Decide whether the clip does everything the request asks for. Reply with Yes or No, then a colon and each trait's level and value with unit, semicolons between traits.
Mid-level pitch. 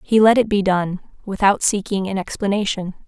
No: high, 200 Hz